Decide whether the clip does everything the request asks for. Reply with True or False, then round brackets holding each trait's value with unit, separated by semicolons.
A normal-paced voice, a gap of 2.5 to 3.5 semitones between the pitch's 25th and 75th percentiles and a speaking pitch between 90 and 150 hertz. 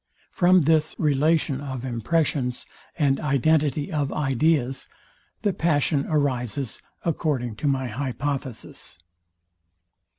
False (95 wpm; 3.0 semitones; 140 Hz)